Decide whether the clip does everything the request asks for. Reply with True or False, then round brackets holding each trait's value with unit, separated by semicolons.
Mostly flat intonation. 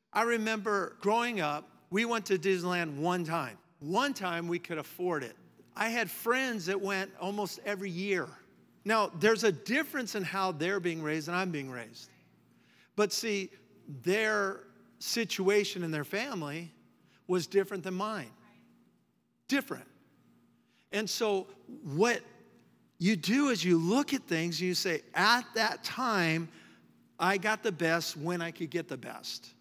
False (4.3 semitones)